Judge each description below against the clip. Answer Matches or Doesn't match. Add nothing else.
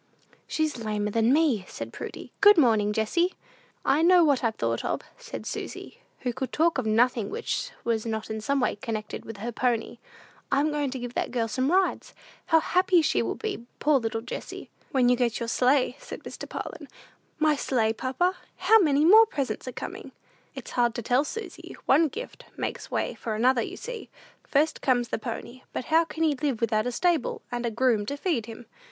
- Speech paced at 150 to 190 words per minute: Doesn't match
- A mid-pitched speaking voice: Doesn't match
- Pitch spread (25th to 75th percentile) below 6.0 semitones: Matches